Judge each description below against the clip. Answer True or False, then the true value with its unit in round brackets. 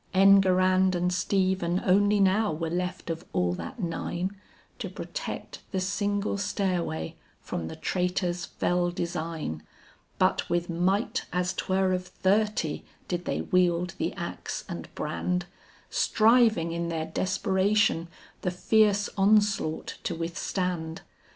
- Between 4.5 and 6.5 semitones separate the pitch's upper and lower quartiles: False (2.4 semitones)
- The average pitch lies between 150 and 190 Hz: True (185 Hz)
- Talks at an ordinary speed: False (125 wpm)